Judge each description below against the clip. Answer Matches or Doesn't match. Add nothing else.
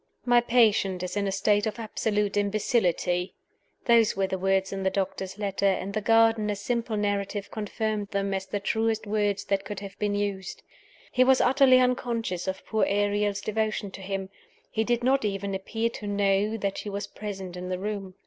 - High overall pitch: Matches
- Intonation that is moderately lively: Doesn't match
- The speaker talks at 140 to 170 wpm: Doesn't match